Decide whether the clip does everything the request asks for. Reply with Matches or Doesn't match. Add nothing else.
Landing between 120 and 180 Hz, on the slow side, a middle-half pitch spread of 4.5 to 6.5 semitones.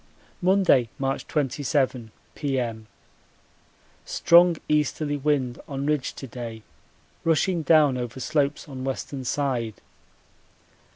Doesn't match